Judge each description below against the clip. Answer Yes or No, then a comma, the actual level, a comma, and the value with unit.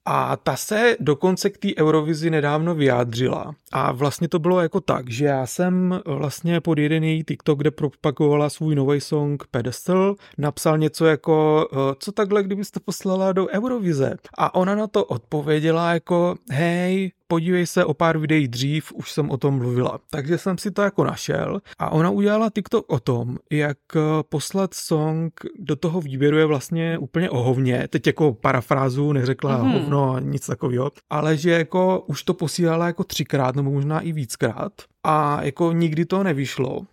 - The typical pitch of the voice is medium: Yes, medium, 155 Hz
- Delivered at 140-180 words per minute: Yes, average, 165 wpm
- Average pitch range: Yes, average, 3.8 semitones